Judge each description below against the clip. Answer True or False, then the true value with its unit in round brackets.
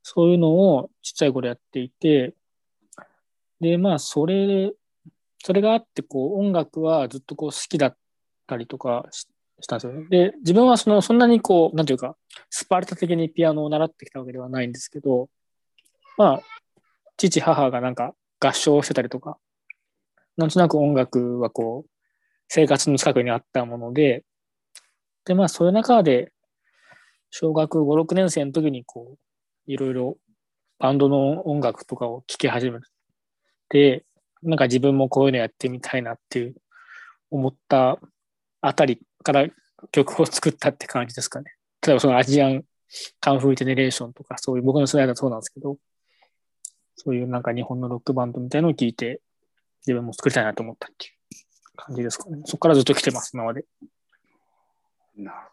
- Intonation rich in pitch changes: False (4.5 semitones)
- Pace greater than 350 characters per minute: False (345 characters per minute)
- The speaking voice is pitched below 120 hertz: False (140 Hz)